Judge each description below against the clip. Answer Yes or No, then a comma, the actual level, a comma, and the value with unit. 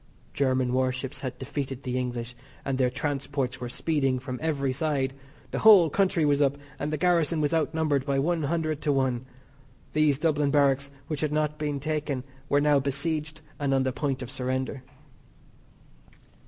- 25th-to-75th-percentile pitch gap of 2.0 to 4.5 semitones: Yes, narrow, 2.6 semitones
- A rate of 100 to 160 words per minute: No, average, 170 wpm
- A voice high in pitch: No, medium, 140 Hz